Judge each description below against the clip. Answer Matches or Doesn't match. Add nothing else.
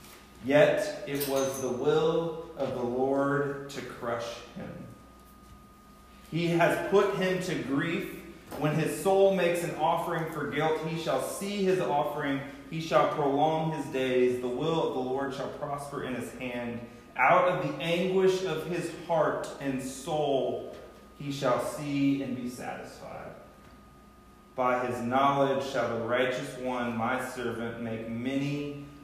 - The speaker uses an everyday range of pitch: Matches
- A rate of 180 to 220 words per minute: Doesn't match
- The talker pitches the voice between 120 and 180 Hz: Matches